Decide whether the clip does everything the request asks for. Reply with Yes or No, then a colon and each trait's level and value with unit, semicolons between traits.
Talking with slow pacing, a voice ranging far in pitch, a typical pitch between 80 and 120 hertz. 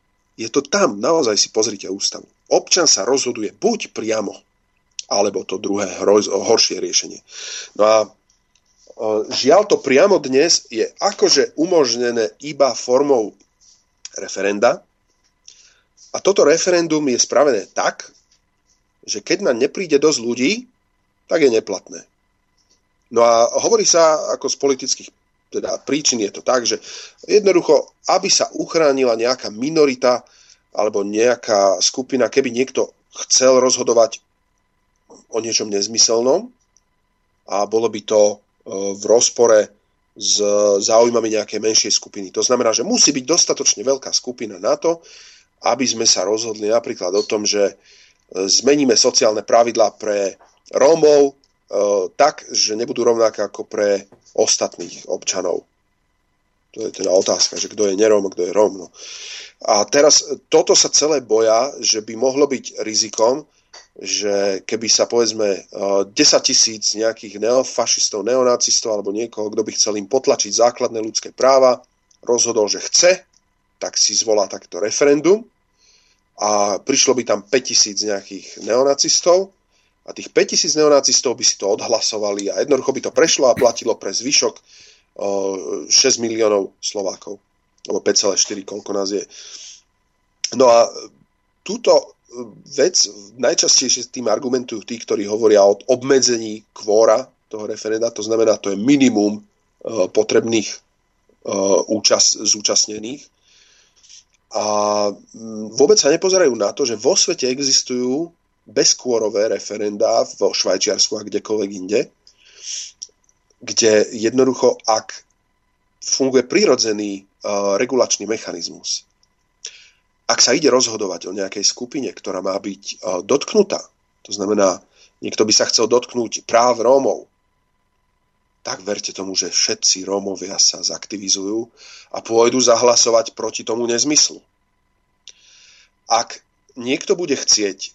No: average, 125 wpm; wide, 6.5 semitones; low, 115 Hz